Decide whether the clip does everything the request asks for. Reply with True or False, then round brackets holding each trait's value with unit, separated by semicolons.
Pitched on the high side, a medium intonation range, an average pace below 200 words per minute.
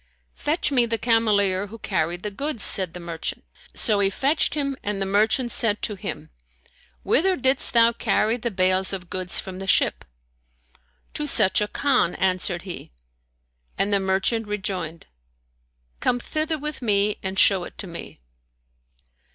True (205 Hz; 4.1 semitones; 160 wpm)